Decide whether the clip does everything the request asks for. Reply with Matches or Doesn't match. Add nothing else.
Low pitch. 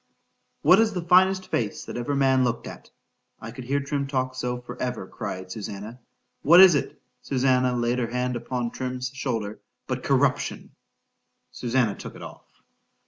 Matches